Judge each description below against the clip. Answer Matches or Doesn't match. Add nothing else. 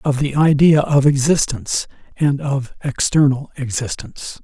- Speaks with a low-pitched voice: Doesn't match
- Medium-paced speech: Doesn't match